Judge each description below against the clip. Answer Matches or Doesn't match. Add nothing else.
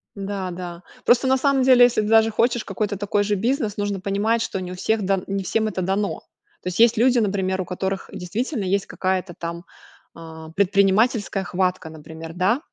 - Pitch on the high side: Matches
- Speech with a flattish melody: Doesn't match